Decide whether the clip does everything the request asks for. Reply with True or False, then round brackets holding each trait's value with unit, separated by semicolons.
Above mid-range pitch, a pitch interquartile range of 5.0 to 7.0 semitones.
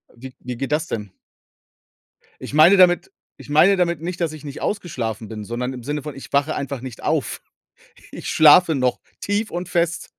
False (150 Hz; 5.4 semitones)